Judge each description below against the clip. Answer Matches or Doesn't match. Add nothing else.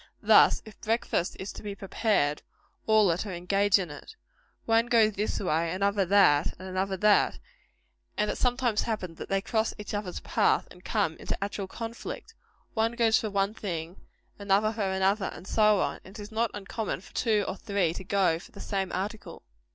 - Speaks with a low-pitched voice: Doesn't match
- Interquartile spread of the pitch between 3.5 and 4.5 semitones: Doesn't match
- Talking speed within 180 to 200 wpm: Matches